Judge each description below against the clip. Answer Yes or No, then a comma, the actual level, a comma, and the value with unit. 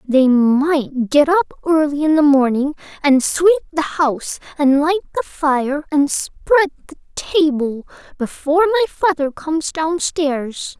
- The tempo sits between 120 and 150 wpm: Yes, average, 140 wpm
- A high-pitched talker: Yes, very high, 300 Hz